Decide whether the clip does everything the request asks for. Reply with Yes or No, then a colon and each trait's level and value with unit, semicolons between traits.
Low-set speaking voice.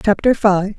No: high, 205 Hz